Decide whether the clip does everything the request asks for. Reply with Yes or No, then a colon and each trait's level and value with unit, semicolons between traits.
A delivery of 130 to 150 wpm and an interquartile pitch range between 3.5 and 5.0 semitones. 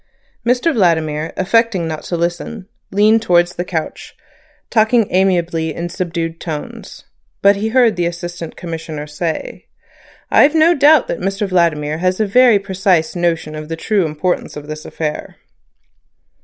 Yes: average, 145 wpm; average, 4.3 semitones